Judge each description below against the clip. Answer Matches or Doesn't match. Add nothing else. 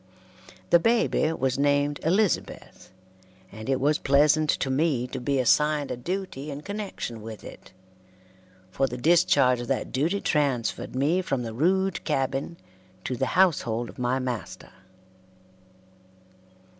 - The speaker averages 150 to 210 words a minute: Doesn't match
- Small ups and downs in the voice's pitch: Doesn't match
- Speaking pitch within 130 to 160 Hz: Matches